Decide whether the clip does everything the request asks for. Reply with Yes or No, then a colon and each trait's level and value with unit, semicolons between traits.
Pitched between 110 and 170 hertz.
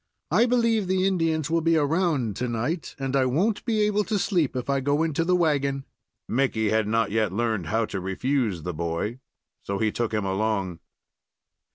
Yes: low, 135 Hz